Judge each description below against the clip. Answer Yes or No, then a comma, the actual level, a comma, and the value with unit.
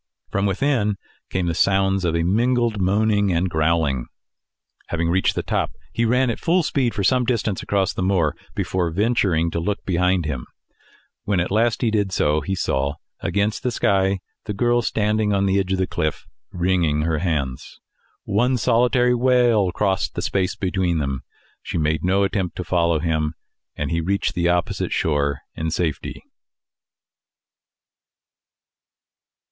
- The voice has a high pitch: No, very low, 95 Hz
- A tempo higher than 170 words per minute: No, average, 155 wpm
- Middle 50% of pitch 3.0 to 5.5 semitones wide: Yes, average, 4.2 semitones